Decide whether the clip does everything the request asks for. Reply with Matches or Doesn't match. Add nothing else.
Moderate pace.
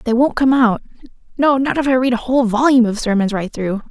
Doesn't match